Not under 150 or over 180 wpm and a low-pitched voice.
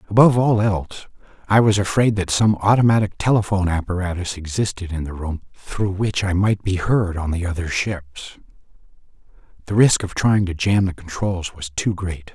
Yes: average, 175 wpm; very low, 95 Hz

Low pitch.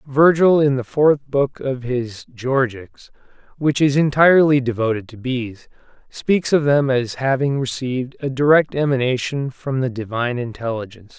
Yes: low, 130 Hz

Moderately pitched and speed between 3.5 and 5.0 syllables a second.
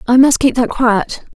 No: high, 245 Hz; 4.5 syllables/s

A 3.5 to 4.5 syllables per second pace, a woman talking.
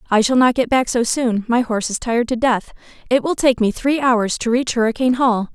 No: 5.7 syllables/s; female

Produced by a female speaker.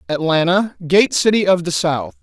No: male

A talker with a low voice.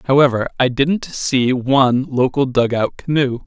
Yes: low, 130 Hz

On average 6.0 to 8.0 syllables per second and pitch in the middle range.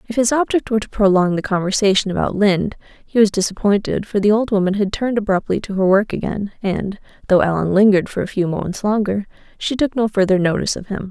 No: 6.4 syllables/s; high, 205 Hz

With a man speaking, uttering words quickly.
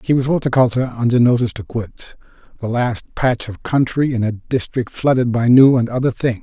No: male; average, 195 wpm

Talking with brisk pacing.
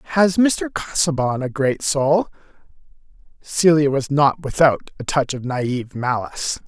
No: slow, 135 wpm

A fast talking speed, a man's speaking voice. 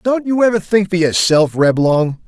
No: average, 185 wpm; male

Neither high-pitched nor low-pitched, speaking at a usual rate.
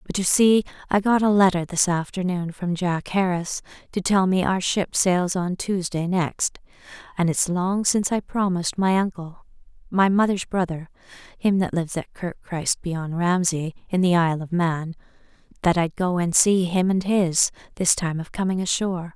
Yes: medium, 180 Hz; average, 180 wpm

